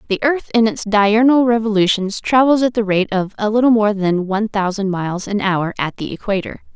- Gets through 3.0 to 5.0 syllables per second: No, 5.4 syllables/s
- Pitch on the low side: No, high, 210 Hz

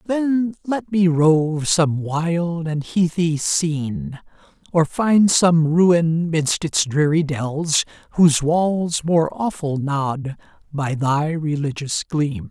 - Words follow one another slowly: Yes, slow, 125 wpm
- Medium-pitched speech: Yes, medium, 160 Hz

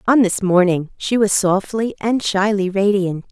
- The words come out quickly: No, average, 165 wpm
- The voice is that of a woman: Yes, female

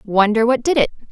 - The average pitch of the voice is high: Yes, high, 230 Hz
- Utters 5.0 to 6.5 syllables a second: Yes, 5.6 syllables/s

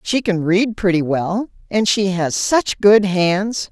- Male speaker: No, female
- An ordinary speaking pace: Yes, average, 180 wpm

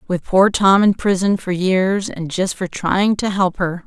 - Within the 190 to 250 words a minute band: Yes, average, 200 wpm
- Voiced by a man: No, female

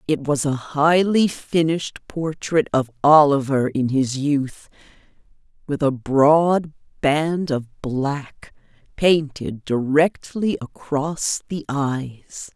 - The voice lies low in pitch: No, medium, 145 Hz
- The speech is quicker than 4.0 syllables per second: No, 3.1 syllables/s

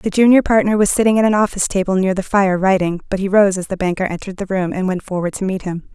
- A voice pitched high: Yes, high, 195 Hz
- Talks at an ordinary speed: No, fast, 285 wpm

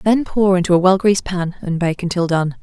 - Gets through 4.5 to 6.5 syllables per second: Yes, 5.6 syllables/s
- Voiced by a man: No, female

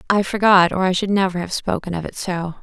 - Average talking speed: No, fast, 250 wpm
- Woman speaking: Yes, female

